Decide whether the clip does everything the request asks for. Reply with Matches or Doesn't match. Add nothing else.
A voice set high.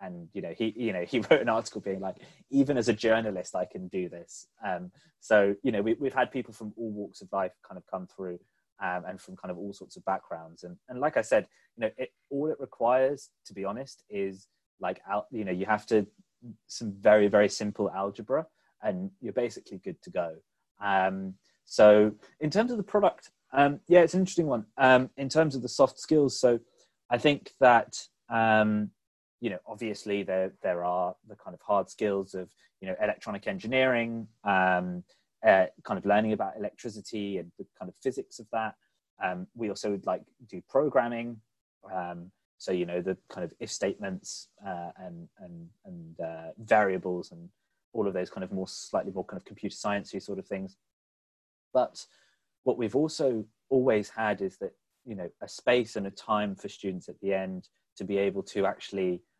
Doesn't match